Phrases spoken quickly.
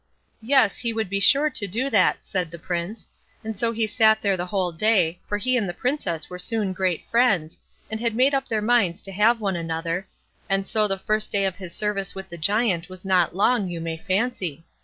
Yes: fast, 220 wpm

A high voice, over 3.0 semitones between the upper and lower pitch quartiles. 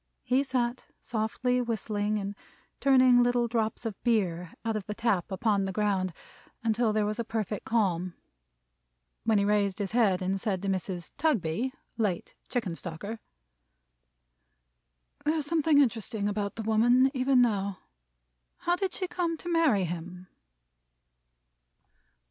Yes: high, 220 Hz; average, 4.0 semitones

